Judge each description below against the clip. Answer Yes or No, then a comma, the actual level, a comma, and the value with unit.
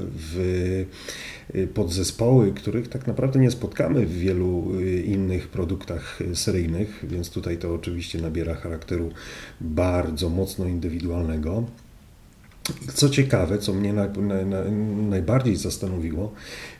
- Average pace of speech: No, slow, 105 wpm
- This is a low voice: Yes, very low, 95 Hz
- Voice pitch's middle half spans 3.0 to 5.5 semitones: Yes, average, 3.3 semitones